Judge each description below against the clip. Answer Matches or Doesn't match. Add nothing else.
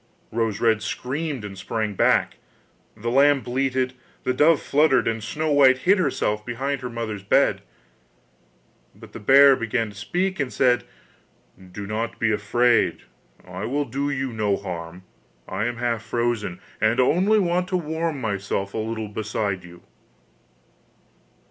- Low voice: Matches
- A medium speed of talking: Matches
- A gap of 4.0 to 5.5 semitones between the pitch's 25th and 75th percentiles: Matches